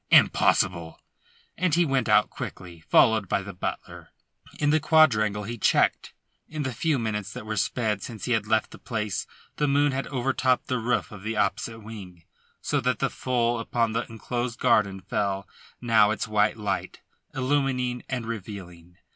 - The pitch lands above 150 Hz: No, low, 115 Hz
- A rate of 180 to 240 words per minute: No, average, 165 wpm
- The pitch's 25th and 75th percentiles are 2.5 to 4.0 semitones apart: Yes, average, 3.5 semitones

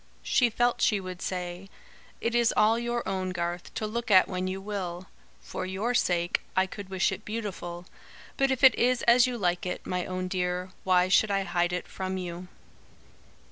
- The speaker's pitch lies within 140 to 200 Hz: Yes, high, 190 Hz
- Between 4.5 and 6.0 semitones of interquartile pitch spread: No, average, 3.7 semitones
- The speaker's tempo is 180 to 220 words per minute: Yes, average, 190 wpm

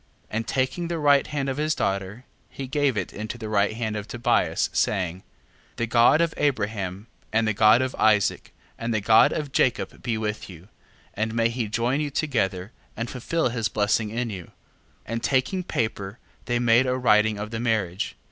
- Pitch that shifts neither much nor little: Yes, average, 3.4 semitones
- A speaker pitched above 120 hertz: No, low, 115 Hz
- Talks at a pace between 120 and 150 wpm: No, average, 195 wpm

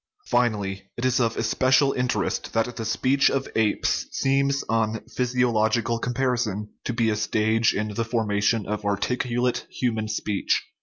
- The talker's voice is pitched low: Yes, low, 115 Hz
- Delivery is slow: No, average, 145 wpm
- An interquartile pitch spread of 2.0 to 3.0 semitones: Yes, narrow, 2.6 semitones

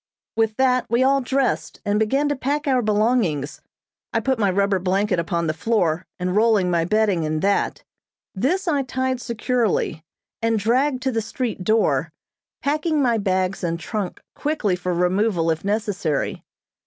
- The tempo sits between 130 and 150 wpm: No, average, 160 wpm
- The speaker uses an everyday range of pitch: No, wide, 5.8 semitones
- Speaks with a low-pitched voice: No, high, 215 Hz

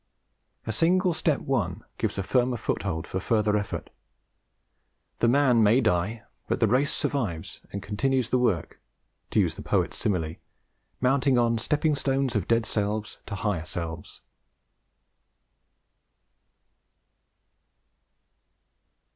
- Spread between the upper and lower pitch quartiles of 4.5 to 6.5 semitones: Yes, average, 4.8 semitones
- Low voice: Yes, low, 115 Hz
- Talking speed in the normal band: No, slow, 120 wpm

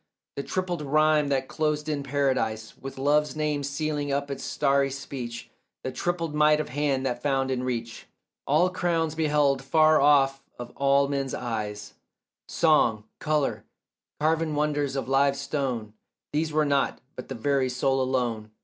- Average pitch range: No, narrow, 2.3 semitones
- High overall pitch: No, medium, 140 Hz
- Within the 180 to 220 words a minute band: No, average, 155 wpm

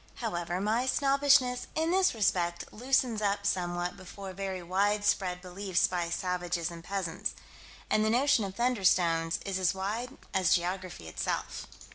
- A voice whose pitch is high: Yes, high, 195 Hz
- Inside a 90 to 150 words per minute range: Yes, average, 140 wpm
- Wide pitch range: No, average, 4.3 semitones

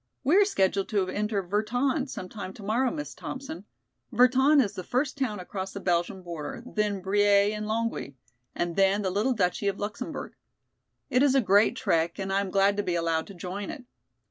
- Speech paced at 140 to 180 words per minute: No, average, 195 wpm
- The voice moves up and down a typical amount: Yes, average, 4.5 semitones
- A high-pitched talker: Yes, high, 205 Hz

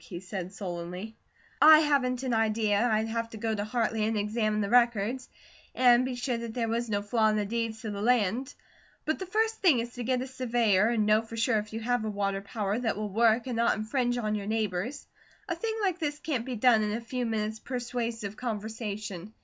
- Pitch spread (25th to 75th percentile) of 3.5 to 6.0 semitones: No, average, 2.7 semitones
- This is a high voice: Yes, high, 225 Hz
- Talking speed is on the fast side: Yes, fast, 220 wpm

